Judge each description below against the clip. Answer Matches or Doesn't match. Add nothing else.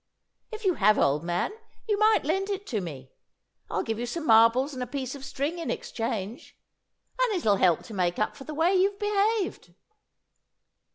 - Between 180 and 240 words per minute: Matches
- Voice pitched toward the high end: Matches